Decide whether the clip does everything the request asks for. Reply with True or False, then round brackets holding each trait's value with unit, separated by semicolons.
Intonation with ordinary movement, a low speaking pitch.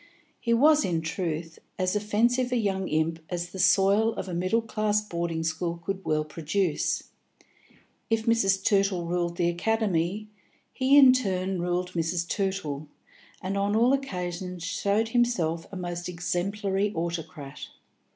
False (3.6 semitones; 185 Hz)